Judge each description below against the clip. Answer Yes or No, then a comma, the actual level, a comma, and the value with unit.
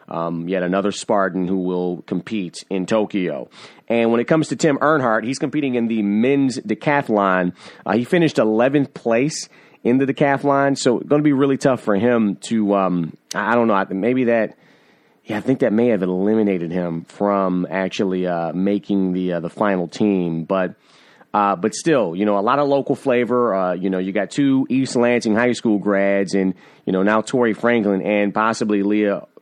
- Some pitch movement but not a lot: Yes, average, 4.4 semitones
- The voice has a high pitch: No, low, 105 Hz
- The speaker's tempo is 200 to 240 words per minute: No, average, 190 wpm